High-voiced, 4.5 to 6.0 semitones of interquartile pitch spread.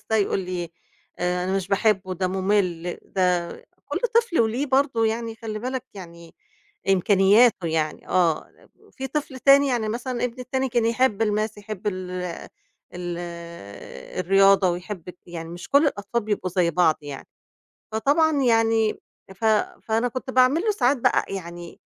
Yes: high, 210 Hz; average, 5.3 semitones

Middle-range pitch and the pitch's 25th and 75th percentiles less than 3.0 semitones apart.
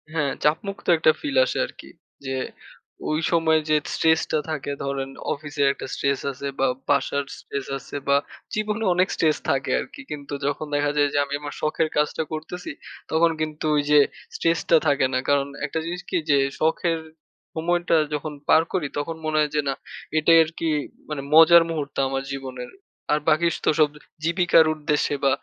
Yes: medium, 155 Hz; narrow, 2.6 semitones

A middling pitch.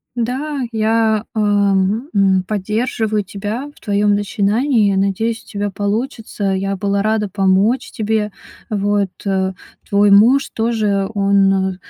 No: high, 205 Hz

